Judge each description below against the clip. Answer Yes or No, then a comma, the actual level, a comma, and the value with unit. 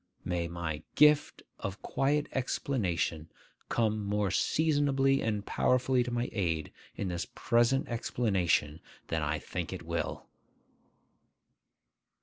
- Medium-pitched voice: No, low, 110 Hz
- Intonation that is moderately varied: No, wide, 7.4 semitones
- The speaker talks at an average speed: No, slow, 115 wpm